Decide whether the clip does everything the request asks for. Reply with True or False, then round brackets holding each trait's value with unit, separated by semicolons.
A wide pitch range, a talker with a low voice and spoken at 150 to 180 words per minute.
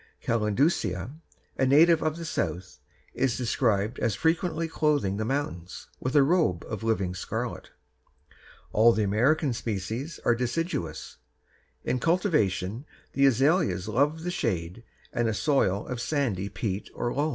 False (6.9 semitones; 120 Hz; 140 wpm)